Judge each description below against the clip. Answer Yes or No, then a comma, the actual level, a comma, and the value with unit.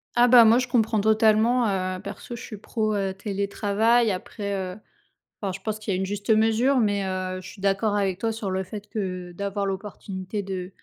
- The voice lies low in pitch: No, high, 205 Hz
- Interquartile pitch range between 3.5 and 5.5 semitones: No, narrow, 2.5 semitones